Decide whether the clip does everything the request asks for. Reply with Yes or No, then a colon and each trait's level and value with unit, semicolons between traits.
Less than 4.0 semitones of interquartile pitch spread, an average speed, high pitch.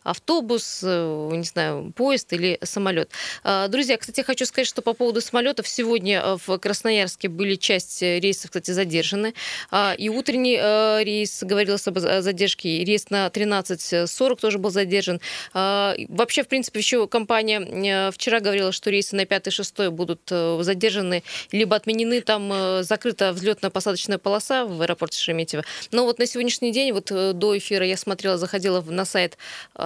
Yes: average, 3.2 semitones; average, 140 wpm; high, 200 Hz